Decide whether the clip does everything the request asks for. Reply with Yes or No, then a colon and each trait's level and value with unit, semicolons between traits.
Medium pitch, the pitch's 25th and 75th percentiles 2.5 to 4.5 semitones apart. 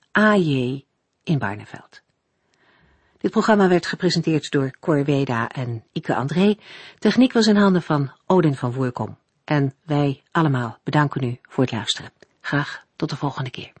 No: medium, 145 Hz; average, 5.3 semitones